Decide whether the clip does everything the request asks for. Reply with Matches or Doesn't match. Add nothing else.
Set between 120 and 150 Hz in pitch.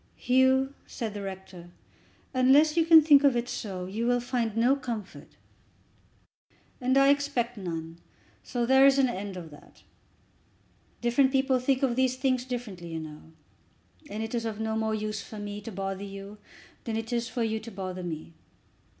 Doesn't match